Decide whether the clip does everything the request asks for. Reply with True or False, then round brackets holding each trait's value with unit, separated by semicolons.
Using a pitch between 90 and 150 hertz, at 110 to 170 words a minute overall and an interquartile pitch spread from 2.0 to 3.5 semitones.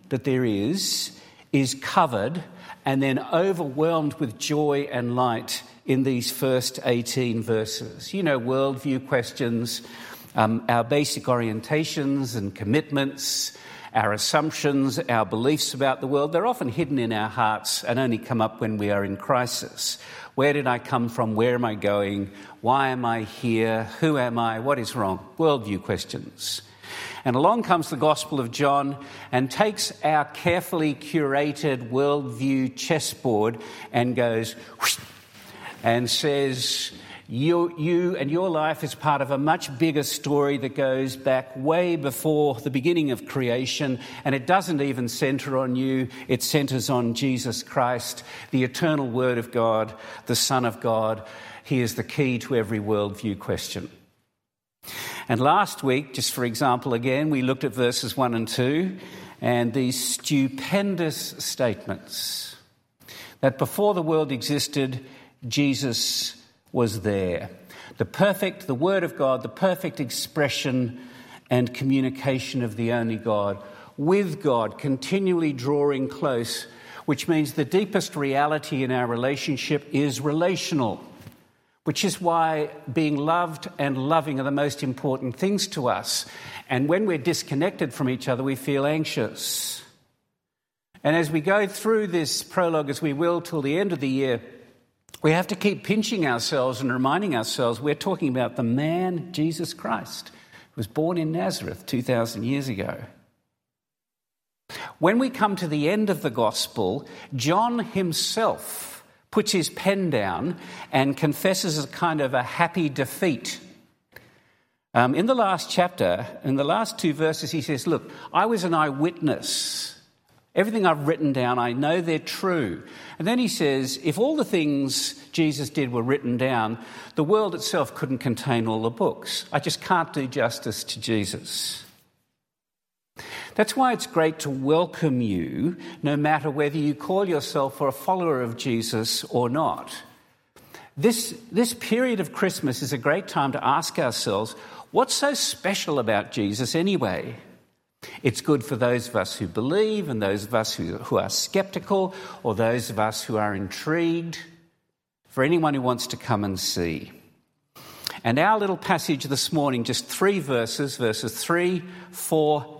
False (140 Hz; 155 wpm; 4.8 semitones)